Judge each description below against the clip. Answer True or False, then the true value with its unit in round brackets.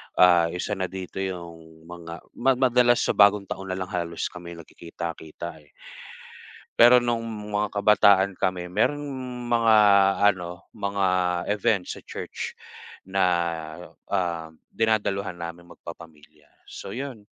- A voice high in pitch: False (95 Hz)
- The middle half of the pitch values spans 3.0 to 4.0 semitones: True (3.6 semitones)